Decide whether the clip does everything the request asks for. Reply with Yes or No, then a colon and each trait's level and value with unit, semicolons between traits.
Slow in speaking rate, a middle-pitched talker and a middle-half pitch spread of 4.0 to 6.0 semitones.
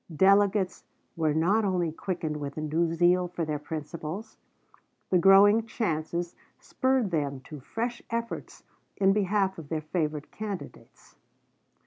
Yes: slow, 130 wpm; medium, 175 Hz; average, 4.5 semitones